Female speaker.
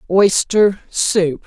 Yes: female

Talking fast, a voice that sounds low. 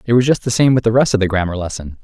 Yes: fast, 355 wpm; low, 110 Hz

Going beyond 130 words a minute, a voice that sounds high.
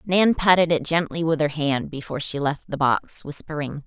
No: average, 200 wpm; medium, 155 Hz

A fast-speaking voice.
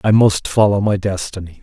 No: average, 185 wpm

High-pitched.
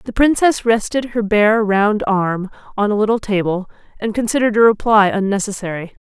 Yes: high, 210 Hz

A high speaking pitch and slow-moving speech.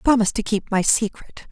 No: high, 220 Hz; average, 200 wpm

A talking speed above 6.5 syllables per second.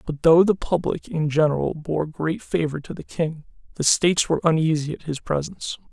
No: 5.4 syllables/s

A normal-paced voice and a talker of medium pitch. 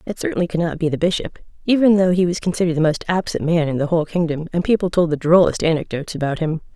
No: fast, 250 wpm; medium, 170 Hz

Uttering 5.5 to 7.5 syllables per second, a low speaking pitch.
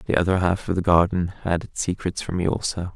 Yes: 5.8 syllables/s; very low, 90 Hz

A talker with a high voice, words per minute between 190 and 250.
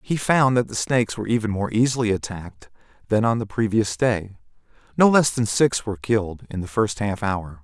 No: low, 110 Hz; fast, 205 wpm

